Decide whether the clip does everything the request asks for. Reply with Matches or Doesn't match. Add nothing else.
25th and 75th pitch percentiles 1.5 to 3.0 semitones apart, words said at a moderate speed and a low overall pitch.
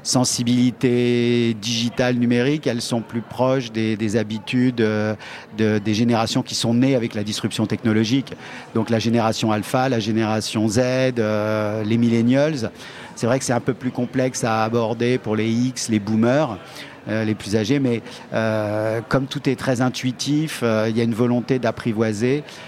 Matches